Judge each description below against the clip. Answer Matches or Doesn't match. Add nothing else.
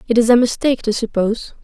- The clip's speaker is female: Matches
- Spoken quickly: Matches